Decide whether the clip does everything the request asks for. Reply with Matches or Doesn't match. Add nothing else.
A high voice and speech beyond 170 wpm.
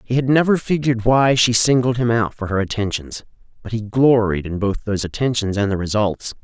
Doesn't match